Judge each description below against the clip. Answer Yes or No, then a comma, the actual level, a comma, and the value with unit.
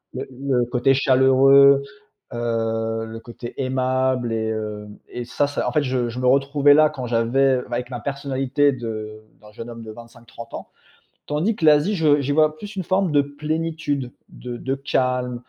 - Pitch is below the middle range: Yes, low, 130 Hz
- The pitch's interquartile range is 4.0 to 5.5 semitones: No, average, 3.3 semitones